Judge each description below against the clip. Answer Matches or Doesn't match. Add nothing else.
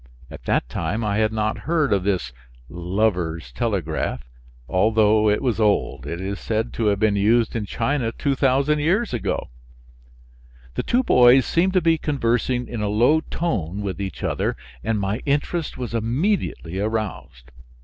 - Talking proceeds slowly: Doesn't match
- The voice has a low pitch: Matches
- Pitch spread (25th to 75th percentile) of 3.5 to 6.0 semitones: Matches